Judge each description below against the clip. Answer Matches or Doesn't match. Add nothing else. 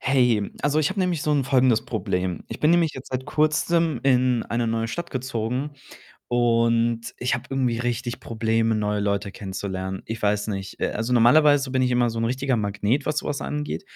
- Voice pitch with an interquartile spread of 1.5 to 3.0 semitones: Doesn't match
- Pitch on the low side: Matches